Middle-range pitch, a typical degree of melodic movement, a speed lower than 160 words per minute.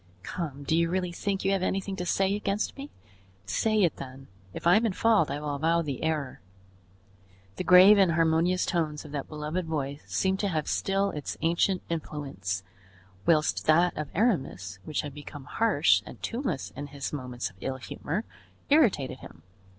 No: medium, 165 Hz; average, 5.0 semitones; average, 180 wpm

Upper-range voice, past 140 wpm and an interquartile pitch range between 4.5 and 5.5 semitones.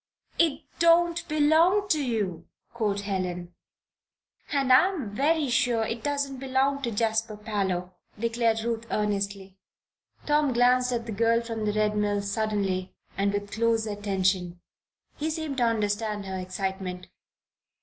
No: high, 225 Hz; slow, 135 wpm; average, 4.9 semitones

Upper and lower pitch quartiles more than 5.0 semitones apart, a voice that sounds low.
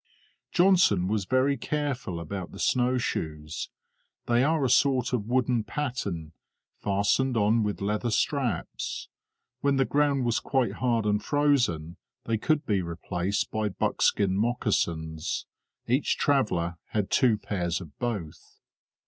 Yes: wide, 5.6 semitones; low, 110 Hz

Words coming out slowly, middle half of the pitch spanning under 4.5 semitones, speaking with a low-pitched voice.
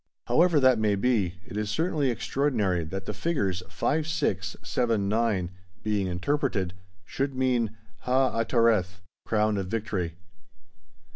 No: slow, 130 wpm; average, 5.1 semitones; low, 110 Hz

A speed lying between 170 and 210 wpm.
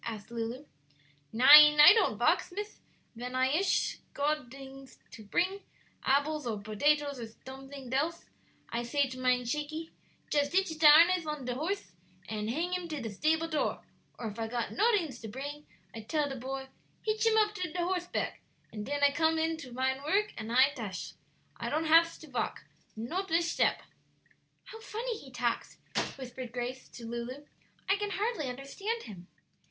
Yes: average, 175 wpm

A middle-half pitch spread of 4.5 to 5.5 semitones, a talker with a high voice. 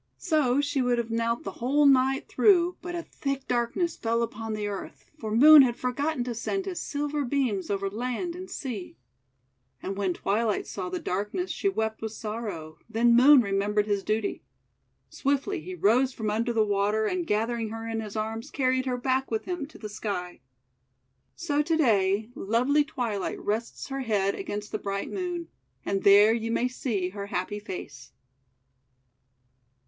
Yes: average, 5.0 semitones; high, 230 Hz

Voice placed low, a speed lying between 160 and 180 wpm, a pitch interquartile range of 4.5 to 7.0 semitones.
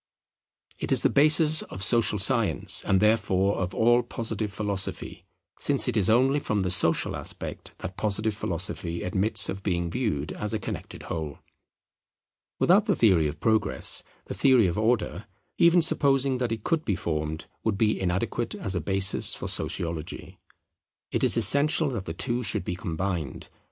Yes: low, 105 Hz; average, 165 wpm; average, 4.9 semitones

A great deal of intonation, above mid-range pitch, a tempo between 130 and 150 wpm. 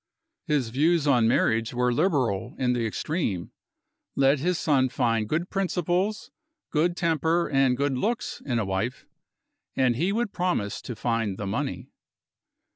No: wide, 6.6 semitones; low, 135 Hz; average, 145 wpm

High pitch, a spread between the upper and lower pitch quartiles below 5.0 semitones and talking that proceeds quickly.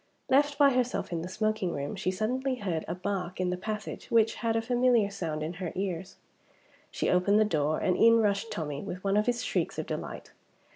Yes: high, 200 Hz; average, 4.2 semitones; fast, 210 wpm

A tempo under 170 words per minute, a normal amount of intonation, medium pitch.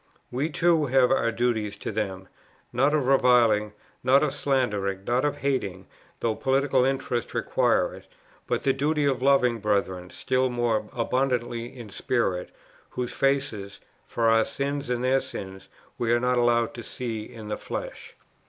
No: average, 160 wpm; average, 3.6 semitones; low, 120 Hz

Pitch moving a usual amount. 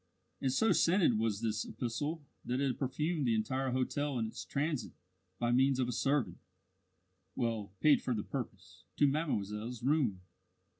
Yes: average, 4.4 semitones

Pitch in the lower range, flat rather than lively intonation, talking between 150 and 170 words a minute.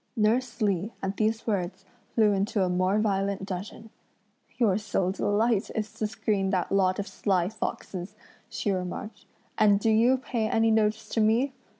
No: high, 210 Hz; narrow, 2.3 semitones; average, 165 wpm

